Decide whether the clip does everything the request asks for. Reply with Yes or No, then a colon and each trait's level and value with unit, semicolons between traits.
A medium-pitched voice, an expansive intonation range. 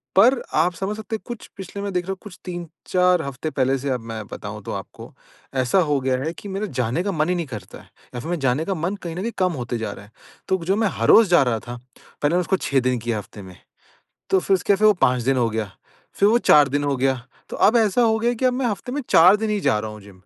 Yes: medium, 175 Hz; wide, 7.7 semitones